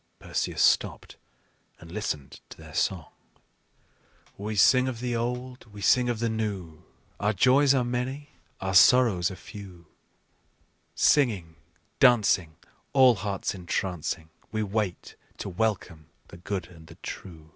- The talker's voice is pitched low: Yes, low, 105 Hz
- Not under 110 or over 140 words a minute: Yes, slow, 135 wpm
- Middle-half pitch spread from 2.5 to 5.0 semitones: No, wide, 5.6 semitones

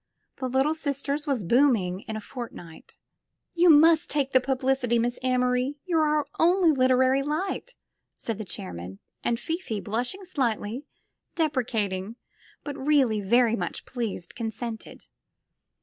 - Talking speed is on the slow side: Yes, slow, 130 wpm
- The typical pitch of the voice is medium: No, very high, 255 Hz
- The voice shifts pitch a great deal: No, average, 4.7 semitones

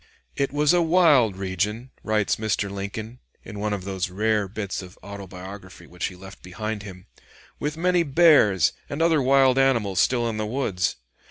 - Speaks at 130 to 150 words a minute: No, average, 170 wpm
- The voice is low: Yes, low, 105 Hz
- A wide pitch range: Yes, wide, 5.7 semitones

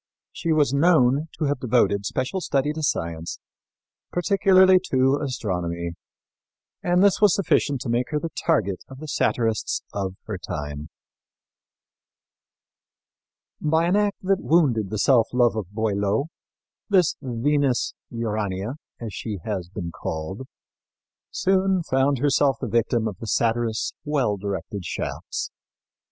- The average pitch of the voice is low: Yes, low, 125 Hz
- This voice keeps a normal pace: No, slow, 130 wpm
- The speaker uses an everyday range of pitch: No, wide, 6.8 semitones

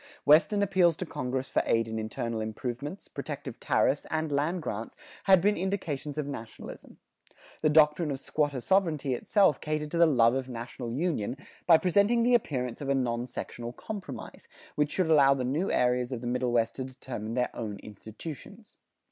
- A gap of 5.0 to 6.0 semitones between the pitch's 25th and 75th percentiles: Yes, wide, 5.4 semitones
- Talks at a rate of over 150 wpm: Yes, average, 175 wpm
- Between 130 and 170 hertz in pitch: Yes, medium, 140 Hz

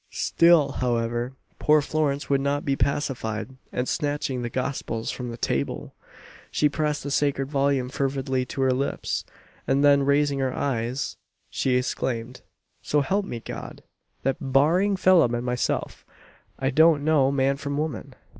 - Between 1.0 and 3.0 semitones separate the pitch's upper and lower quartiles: Yes, narrow, 2.4 semitones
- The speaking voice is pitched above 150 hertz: No, low, 135 Hz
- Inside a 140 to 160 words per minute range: Yes, average, 150 wpm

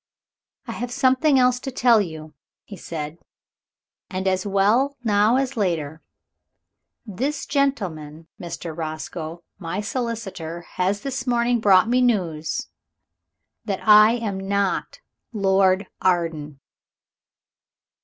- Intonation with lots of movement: Yes, wide, 6.2 semitones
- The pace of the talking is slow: Yes, slow, 110 wpm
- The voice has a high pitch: Yes, high, 200 Hz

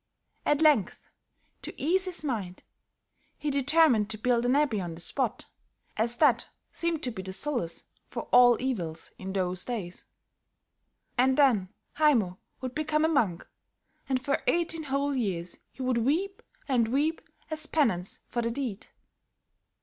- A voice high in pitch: Yes, very high, 250 Hz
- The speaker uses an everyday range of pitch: No, wide, 6.4 semitones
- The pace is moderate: Yes, average, 150 wpm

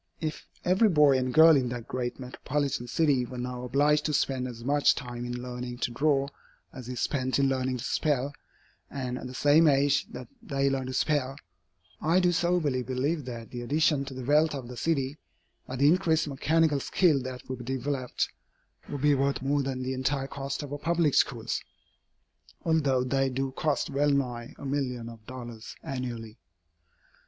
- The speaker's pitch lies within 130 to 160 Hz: Yes, low, 135 Hz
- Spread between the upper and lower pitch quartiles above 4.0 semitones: No, narrow, 2.6 semitones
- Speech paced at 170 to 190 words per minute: Yes, average, 185 wpm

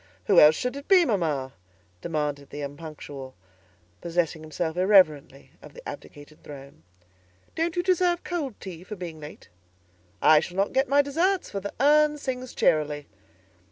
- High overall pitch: No, medium, 175 Hz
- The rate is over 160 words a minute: No, average, 155 wpm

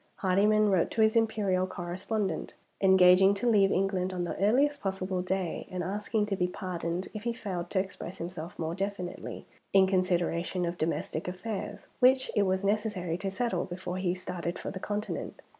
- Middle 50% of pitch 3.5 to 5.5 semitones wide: No, narrow, 2.4 semitones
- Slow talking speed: No, average, 175 wpm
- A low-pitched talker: No, high, 190 Hz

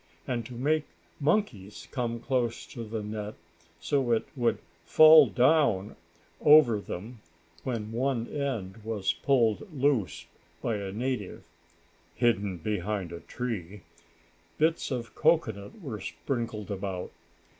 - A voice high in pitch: No, low, 115 Hz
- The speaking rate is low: Yes, slow, 120 wpm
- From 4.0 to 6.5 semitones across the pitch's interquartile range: Yes, average, 4.6 semitones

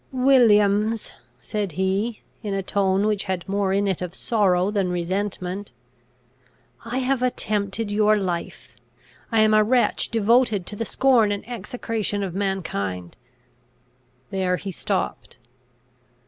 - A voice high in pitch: Yes, high, 205 Hz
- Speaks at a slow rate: Yes, slow, 130 wpm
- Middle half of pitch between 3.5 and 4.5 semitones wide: No, narrow, 2.5 semitones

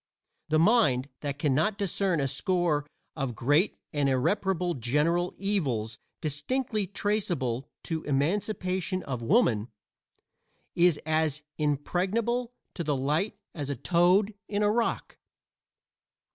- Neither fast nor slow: No, slow, 115 wpm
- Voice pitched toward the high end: No, medium, 165 Hz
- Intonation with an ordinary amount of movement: No, wide, 5.8 semitones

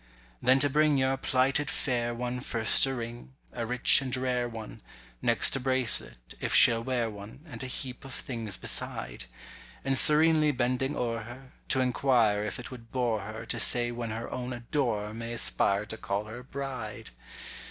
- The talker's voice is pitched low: Yes, low, 120 Hz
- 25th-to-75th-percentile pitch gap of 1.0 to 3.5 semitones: Yes, narrow, 2.5 semitones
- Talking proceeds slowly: No, average, 175 wpm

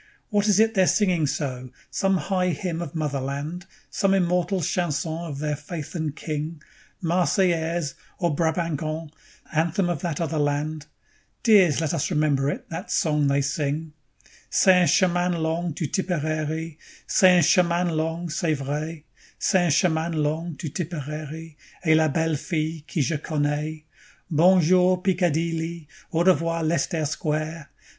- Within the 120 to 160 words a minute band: Yes, average, 140 wpm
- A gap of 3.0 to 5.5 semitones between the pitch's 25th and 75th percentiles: No, narrow, 2.5 semitones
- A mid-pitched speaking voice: Yes, medium, 160 Hz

